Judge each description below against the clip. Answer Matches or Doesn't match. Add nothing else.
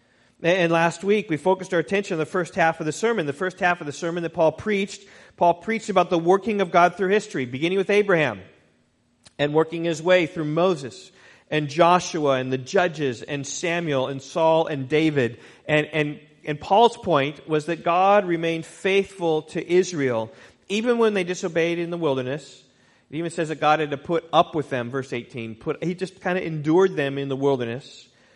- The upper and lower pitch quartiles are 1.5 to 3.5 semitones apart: Doesn't match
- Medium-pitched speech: Matches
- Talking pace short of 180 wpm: Doesn't match